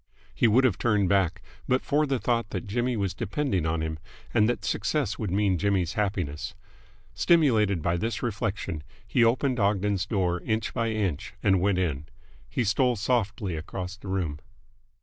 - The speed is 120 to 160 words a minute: No, average, 170 wpm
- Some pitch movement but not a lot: Yes, average, 4.2 semitones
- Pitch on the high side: No, low, 100 Hz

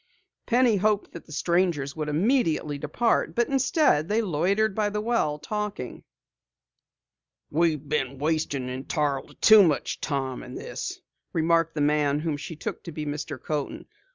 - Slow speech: No, average, 150 wpm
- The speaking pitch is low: No, medium, 155 Hz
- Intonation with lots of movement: Yes, wide, 6.0 semitones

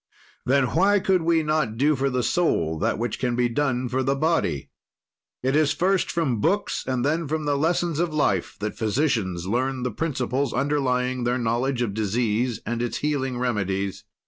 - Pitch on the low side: Yes, low, 130 Hz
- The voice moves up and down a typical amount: Yes, average, 4.3 semitones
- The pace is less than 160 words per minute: No, average, 175 wpm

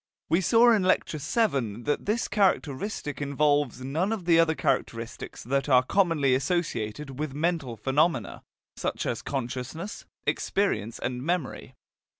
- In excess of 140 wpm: No, slow, 135 wpm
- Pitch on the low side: No, medium, 145 Hz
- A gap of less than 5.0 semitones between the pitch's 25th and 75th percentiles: No, average, 5.3 semitones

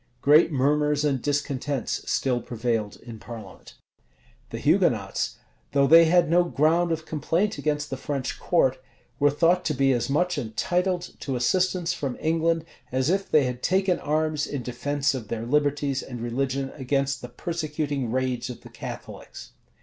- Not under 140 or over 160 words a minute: Yes, average, 155 wpm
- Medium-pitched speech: Yes, medium, 145 Hz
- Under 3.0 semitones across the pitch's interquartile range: No, average, 4.0 semitones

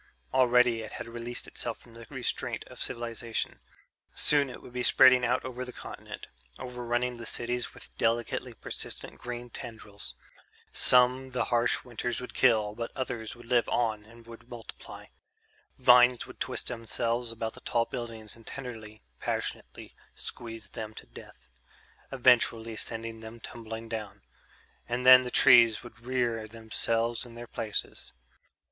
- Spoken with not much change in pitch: Yes, narrow, 1.5 semitones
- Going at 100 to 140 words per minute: No, average, 150 wpm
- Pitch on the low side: Yes, low, 120 Hz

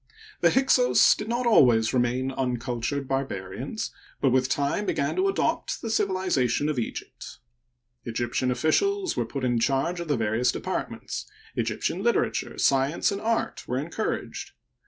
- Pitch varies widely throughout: Yes, wide, 8.2 semitones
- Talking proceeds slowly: No, average, 150 wpm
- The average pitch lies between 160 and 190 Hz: No, low, 135 Hz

